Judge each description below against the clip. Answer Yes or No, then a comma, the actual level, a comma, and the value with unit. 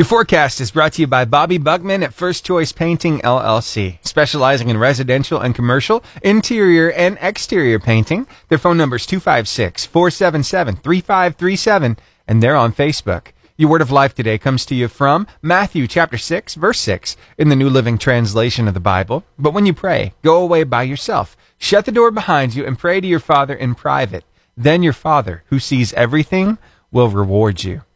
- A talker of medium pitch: Yes, medium, 145 Hz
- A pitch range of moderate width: No, wide, 6.3 semitones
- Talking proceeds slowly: No, average, 180 wpm